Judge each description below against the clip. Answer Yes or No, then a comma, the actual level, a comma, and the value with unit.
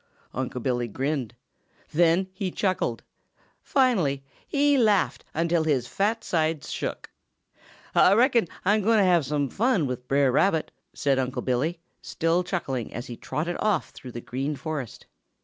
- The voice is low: No, medium, 160 Hz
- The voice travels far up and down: Yes, wide, 6.6 semitones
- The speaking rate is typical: Yes, average, 150 wpm